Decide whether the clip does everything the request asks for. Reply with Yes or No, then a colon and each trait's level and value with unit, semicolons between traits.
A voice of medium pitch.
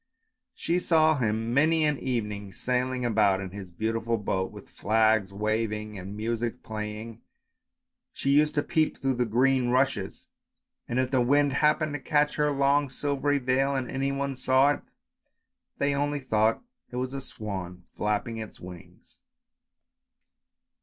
No: low, 125 Hz